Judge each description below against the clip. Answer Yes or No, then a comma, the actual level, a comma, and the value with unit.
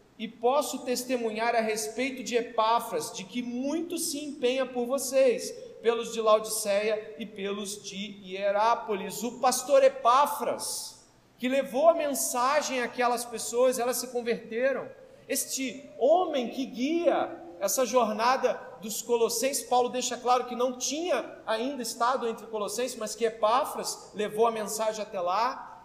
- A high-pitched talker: Yes, high, 245 Hz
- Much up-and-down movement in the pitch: No, average, 3.0 semitones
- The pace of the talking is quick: No, average, 135 wpm